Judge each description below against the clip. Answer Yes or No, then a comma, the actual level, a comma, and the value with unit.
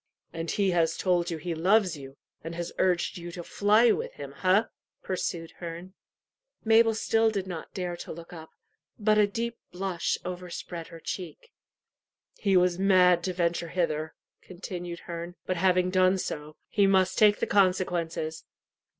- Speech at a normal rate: Yes, average, 160 wpm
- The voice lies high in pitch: No, medium, 180 Hz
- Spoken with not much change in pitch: Yes, narrow, 2.3 semitones